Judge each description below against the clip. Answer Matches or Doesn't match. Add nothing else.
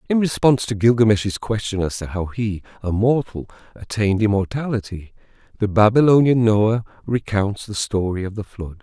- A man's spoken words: Matches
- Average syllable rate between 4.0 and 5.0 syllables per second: Doesn't match